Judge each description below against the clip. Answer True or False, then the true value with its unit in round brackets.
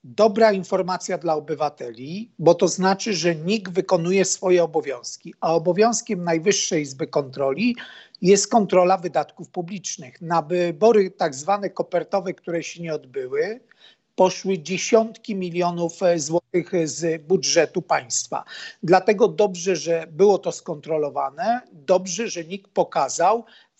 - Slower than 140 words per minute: True (120 wpm)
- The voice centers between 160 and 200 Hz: True (185 Hz)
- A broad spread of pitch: False (3.3 semitones)